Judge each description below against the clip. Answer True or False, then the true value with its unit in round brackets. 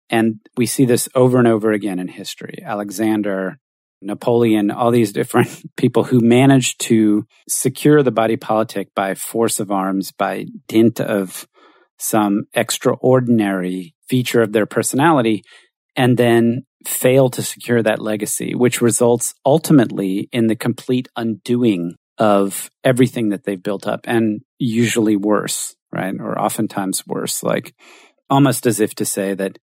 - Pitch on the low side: True (110 Hz)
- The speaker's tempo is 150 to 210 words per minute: False (140 wpm)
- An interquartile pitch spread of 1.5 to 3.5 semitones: True (2.9 semitones)